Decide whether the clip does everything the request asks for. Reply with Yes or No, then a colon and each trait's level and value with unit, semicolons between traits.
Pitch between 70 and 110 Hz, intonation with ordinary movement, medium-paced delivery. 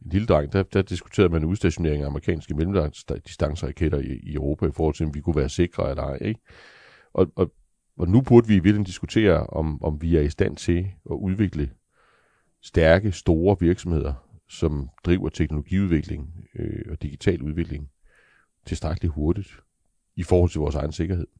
Yes: very low, 85 Hz; average, 3.7 semitones; average, 170 wpm